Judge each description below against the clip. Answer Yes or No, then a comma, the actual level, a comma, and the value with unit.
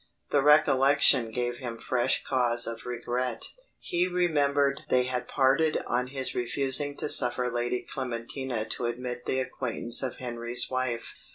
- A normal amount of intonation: No, narrow, 2.2 semitones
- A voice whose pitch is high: No, low, 125 Hz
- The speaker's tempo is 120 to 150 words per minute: Yes, average, 145 wpm